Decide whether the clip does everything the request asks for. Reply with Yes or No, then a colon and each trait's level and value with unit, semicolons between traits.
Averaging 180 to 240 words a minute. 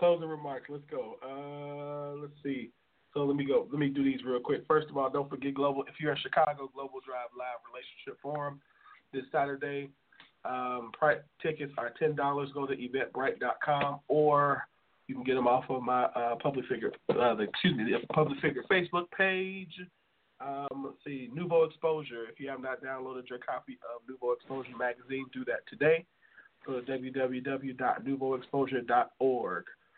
No: average, 165 wpm